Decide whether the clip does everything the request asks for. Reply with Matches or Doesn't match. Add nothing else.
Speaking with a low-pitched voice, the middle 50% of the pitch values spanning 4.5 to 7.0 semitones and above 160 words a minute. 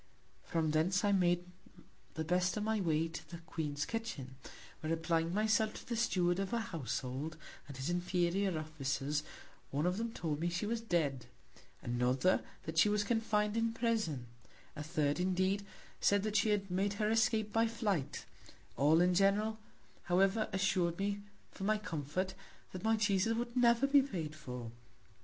Doesn't match